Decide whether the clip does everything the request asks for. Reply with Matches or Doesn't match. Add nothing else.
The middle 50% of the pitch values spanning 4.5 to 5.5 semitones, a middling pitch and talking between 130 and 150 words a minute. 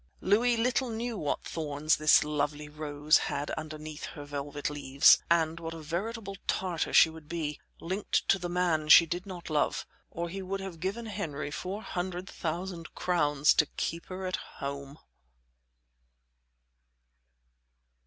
Doesn't match